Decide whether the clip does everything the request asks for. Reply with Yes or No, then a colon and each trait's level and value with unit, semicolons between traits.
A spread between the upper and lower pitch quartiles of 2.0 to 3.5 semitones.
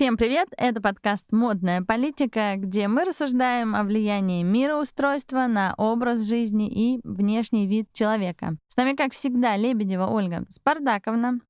Yes: average, 3.2 semitones